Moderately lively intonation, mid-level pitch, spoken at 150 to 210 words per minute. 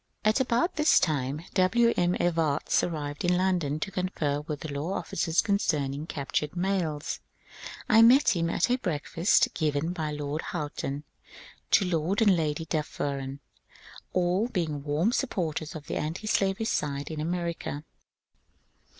No: average, 4.2 semitones; medium, 165 Hz; average, 140 wpm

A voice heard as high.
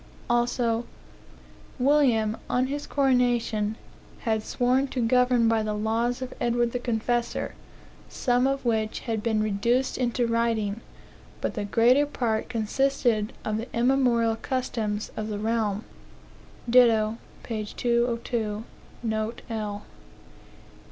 Yes: high, 235 Hz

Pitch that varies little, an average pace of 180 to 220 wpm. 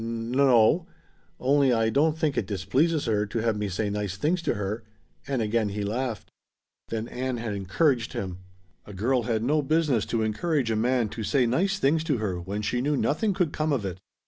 No: average, 5.2 semitones; fast, 205 wpm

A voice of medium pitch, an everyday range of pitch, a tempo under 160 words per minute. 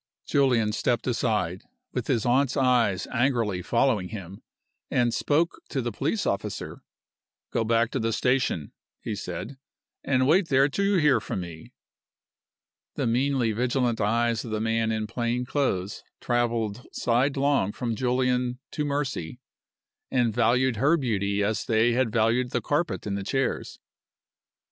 No: low, 120 Hz; average, 3.2 semitones; average, 145 wpm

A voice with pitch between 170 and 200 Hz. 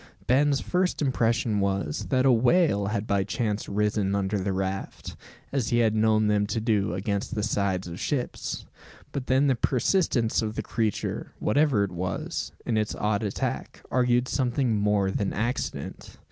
No: low, 110 Hz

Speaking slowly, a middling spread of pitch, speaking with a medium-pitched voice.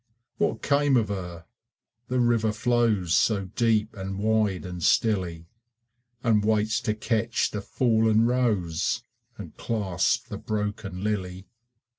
No: slow, 125 wpm; average, 3.1 semitones; low, 105 Hz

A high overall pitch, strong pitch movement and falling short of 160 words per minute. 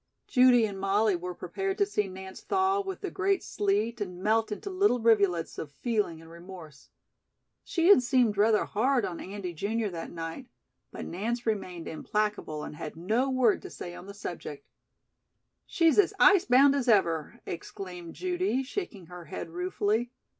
No: high, 210 Hz; wide, 6.4 semitones; average, 170 wpm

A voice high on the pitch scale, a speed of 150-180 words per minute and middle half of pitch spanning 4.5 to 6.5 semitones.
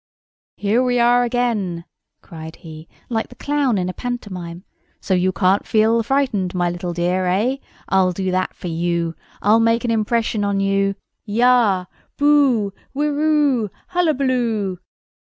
No: high, 210 Hz; slow, 135 wpm; average, 5.1 semitones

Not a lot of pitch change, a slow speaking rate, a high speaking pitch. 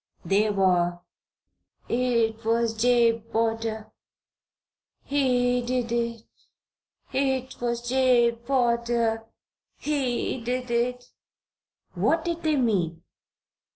Yes: narrow, 1.9 semitones; slow, 85 wpm; high, 235 Hz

